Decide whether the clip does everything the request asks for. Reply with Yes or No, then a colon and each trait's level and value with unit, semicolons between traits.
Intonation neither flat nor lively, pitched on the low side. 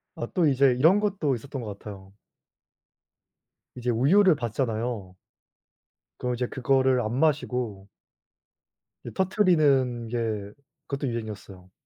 Yes: average, 4.3 semitones; low, 125 Hz